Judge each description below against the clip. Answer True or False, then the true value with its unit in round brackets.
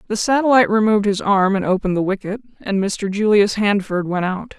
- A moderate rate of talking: True (195 wpm)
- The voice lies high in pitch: True (205 Hz)